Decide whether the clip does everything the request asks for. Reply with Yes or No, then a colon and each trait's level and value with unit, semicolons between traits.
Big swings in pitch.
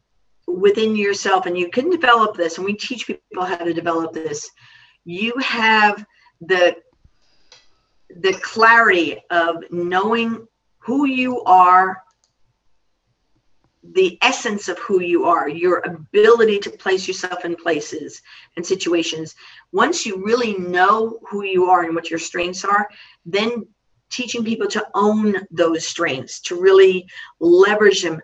No: average, 5.0 semitones